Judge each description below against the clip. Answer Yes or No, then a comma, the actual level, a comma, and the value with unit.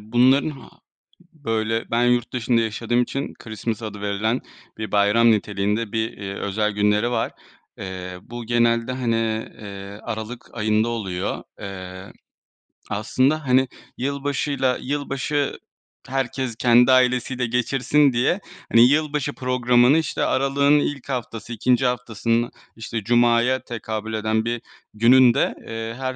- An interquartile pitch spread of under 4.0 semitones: Yes, average, 2.9 semitones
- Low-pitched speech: Yes, low, 120 Hz